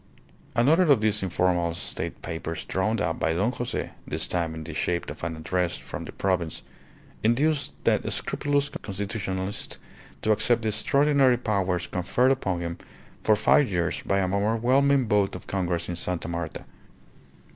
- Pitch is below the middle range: Yes, low, 100 Hz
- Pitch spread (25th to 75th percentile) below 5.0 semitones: No, wide, 5.6 semitones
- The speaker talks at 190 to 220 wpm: No, average, 155 wpm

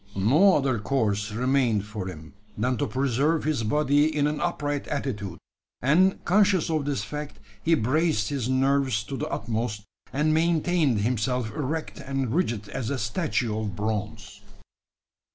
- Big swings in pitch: Yes, wide, 5.7 semitones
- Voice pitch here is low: Yes, low, 130 Hz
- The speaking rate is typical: Yes, average, 150 wpm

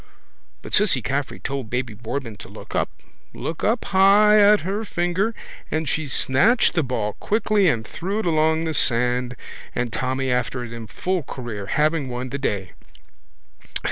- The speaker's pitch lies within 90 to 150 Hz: Yes, medium, 140 Hz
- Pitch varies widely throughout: Yes, wide, 7.3 semitones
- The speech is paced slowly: No, average, 165 wpm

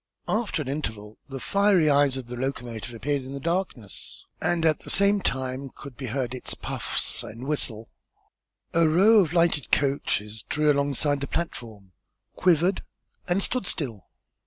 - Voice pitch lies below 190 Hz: Yes, medium, 140 Hz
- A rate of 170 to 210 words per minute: No, average, 160 wpm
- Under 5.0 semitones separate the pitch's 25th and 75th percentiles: No, average, 5.3 semitones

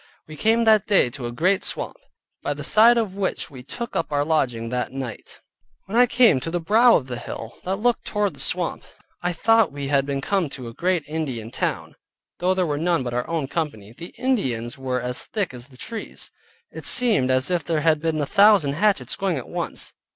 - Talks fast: Yes, fast, 220 wpm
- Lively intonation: Yes, wide, 7.4 semitones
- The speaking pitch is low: No, medium, 160 Hz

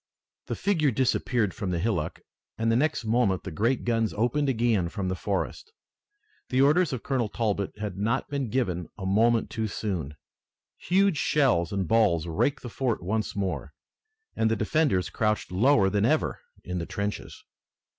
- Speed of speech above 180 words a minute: No, average, 165 wpm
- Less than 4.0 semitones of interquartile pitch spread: No, average, 4.9 semitones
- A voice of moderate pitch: No, low, 110 Hz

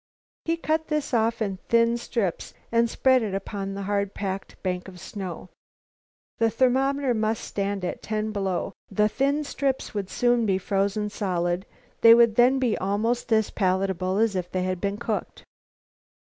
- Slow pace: No, average, 165 wpm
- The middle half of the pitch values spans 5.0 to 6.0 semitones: No, average, 3.5 semitones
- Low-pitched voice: No, high, 210 Hz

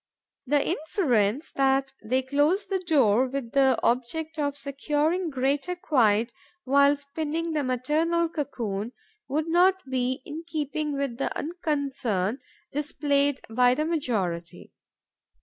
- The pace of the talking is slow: Yes, slow, 120 wpm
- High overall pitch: Yes, very high, 280 Hz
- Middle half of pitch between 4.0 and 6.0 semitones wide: No, average, 3.6 semitones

